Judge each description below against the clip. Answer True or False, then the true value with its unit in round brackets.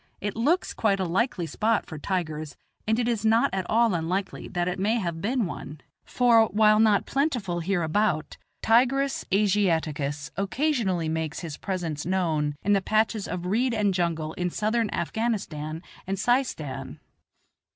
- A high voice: True (195 Hz)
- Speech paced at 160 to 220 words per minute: False (150 wpm)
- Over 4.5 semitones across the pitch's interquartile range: True (5.0 semitones)